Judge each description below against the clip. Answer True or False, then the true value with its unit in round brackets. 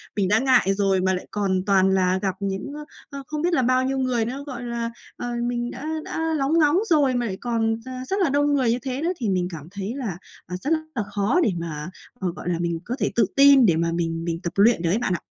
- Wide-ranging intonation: True (6.0 semitones)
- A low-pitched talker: False (230 Hz)